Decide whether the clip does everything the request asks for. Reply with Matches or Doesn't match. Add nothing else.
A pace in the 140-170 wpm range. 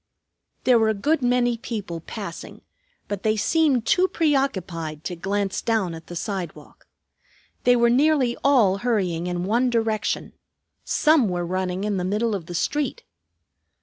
Matches